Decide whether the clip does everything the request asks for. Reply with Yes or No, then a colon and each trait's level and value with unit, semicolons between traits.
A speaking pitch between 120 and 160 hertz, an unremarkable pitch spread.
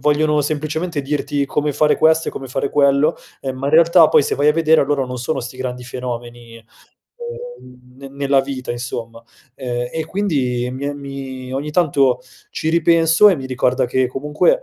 Yes: medium, 140 Hz; average, 3.2 semitones